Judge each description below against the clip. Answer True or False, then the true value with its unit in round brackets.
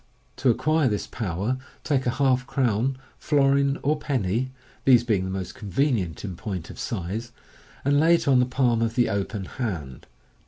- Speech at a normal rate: True (170 wpm)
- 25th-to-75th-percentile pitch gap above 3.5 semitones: True (5.4 semitones)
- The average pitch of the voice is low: True (120 Hz)